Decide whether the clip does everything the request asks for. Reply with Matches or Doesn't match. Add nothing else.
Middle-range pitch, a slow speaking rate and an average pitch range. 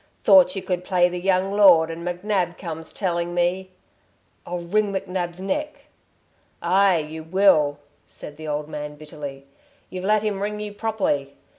Doesn't match